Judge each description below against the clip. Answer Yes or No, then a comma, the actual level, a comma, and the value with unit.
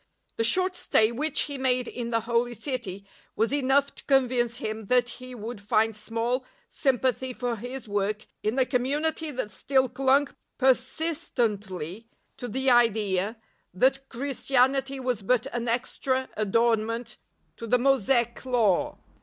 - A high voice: Yes, high, 245 Hz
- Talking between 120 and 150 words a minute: Yes, average, 145 wpm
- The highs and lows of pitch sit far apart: No, average, 2.9 semitones